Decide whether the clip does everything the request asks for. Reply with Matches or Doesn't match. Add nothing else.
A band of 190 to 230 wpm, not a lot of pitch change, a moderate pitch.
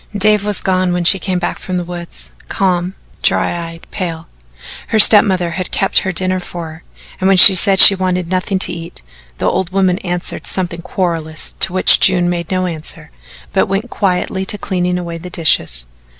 Matches